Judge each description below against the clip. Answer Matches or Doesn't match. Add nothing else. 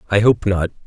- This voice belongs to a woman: Doesn't match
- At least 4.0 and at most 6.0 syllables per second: Matches